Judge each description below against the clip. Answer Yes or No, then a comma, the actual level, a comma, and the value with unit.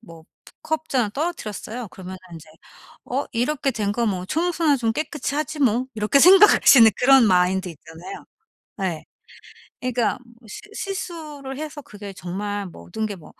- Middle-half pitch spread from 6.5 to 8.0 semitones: Yes, wide, 7.1 semitones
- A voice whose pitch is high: Yes, high, 235 Hz